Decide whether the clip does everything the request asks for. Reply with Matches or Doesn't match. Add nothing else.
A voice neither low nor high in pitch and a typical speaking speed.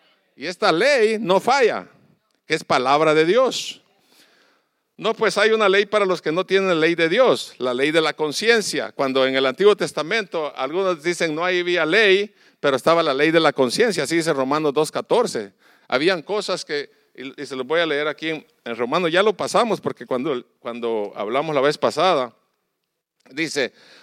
Matches